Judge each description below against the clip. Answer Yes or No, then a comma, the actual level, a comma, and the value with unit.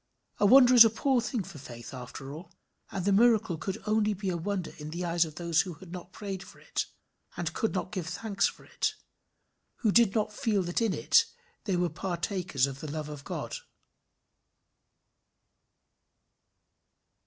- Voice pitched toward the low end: No, medium, 185 Hz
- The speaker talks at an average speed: Yes, average, 175 wpm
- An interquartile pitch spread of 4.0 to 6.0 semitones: Yes, average, 4.6 semitones